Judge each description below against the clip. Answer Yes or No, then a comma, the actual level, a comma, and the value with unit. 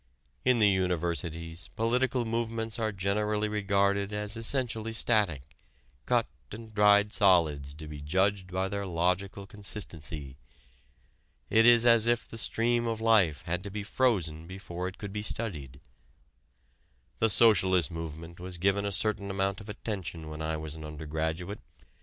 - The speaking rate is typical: Yes, average, 145 wpm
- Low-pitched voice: Yes, low, 100 Hz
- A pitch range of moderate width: Yes, average, 4.6 semitones